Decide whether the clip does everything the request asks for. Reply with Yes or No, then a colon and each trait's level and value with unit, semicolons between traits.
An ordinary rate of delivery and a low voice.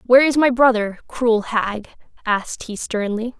No: average, 160 wpm; high, 230 Hz